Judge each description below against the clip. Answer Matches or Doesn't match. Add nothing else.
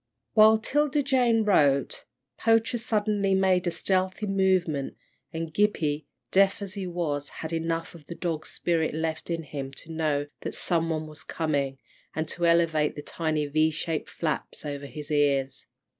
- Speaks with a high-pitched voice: Doesn't match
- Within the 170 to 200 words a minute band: Doesn't match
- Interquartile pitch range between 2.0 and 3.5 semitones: Doesn't match